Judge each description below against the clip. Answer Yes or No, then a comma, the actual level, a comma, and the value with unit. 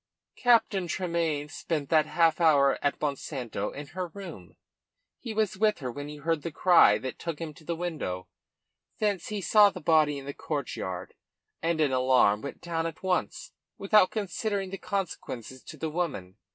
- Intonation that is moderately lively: Yes, average, 4.6 semitones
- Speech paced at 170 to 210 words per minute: Yes, average, 175 wpm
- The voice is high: No, medium, 160 Hz